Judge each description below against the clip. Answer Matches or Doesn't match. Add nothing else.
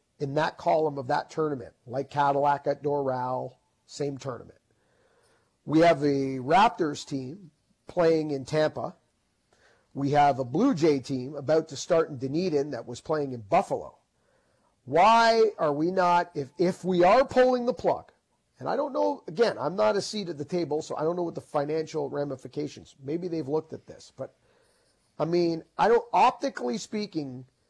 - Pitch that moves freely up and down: Doesn't match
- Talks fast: Doesn't match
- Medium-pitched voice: Matches